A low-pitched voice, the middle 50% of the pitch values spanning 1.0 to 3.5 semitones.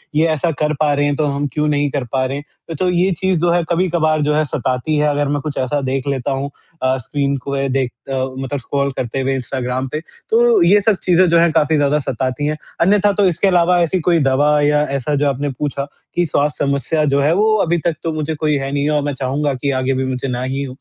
No: medium, 145 Hz; average, 3.1 semitones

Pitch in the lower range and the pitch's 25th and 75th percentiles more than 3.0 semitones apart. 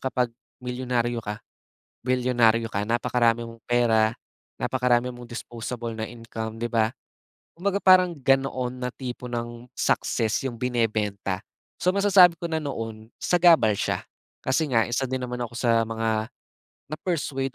No: low, 120 Hz; narrow, 2.5 semitones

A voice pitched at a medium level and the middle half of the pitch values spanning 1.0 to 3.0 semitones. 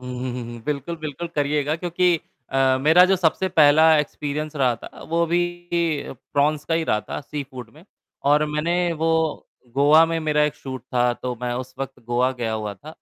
No: medium, 150 Hz; average, 3.8 semitones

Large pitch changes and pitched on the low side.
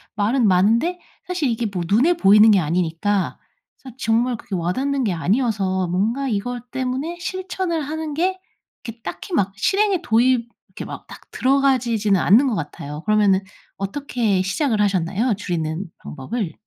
No: wide, 5.8 semitones; high, 225 Hz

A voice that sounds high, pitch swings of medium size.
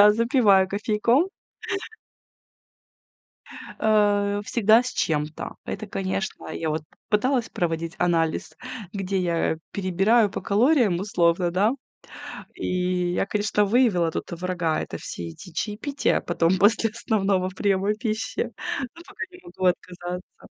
Yes: high, 195 Hz; average, 3.6 semitones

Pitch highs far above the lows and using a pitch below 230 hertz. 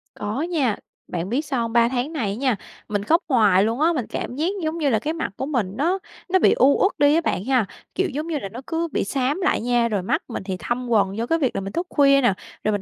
No: wide, 6.2 semitones; very high, 255 Hz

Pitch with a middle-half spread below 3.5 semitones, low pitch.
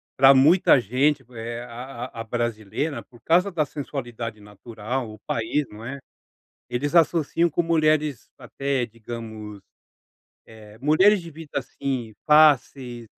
No: average, 4.6 semitones; low, 130 Hz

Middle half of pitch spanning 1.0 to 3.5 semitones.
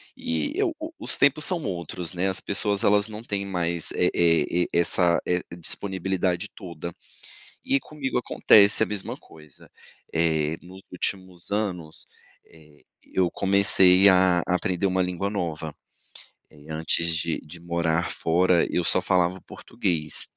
Yes: average, 3.0 semitones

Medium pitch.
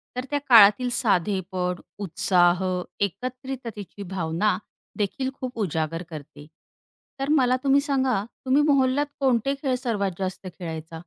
No: high, 210 Hz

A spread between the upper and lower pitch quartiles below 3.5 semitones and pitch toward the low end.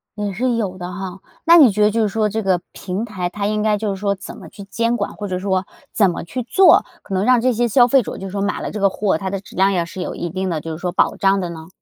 No: average, 2.7 semitones; high, 200 Hz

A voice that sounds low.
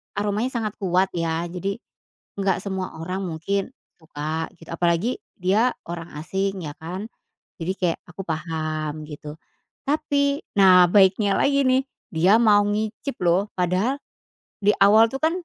No: high, 190 Hz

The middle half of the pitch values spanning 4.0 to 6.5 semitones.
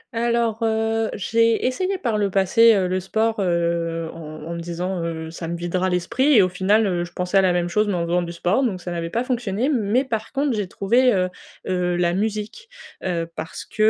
Yes: average, 4.6 semitones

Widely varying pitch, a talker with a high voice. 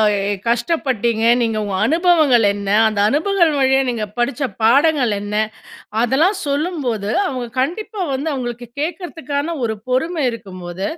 Yes: wide, 6.0 semitones; very high, 265 Hz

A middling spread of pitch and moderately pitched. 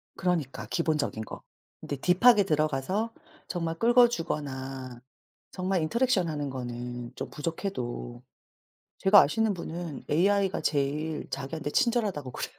No: wide, 6.1 semitones; medium, 160 Hz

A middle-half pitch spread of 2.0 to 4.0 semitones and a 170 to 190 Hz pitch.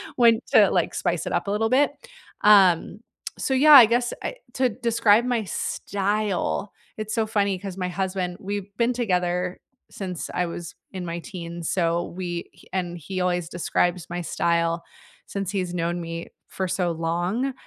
Yes: average, 3.6 semitones; medium, 185 Hz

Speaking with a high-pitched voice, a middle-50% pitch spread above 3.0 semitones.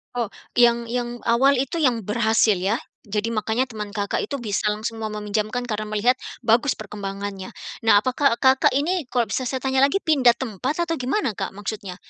Yes: high, 230 Hz; average, 3.5 semitones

